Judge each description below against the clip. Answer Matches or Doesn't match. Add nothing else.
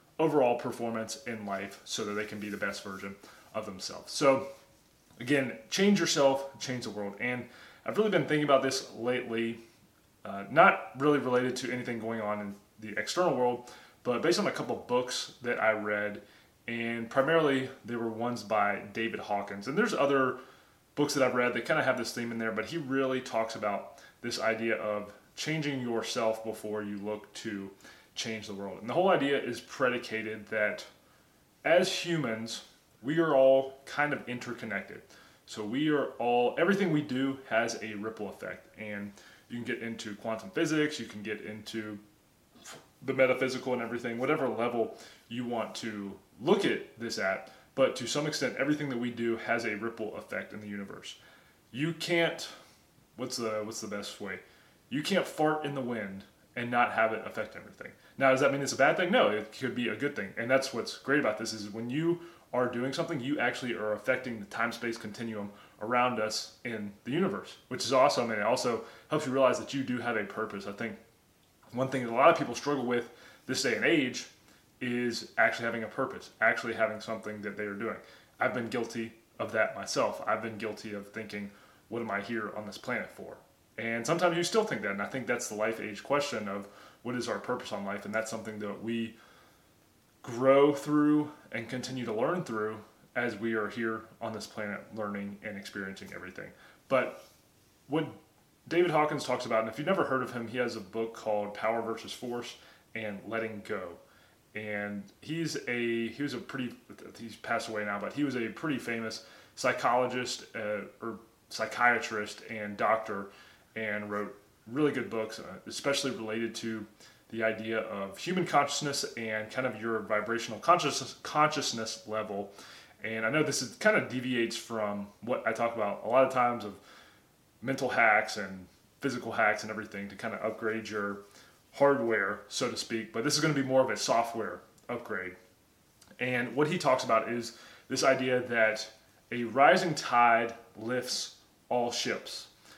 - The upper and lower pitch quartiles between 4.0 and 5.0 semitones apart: Doesn't match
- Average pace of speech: Matches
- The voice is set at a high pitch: Doesn't match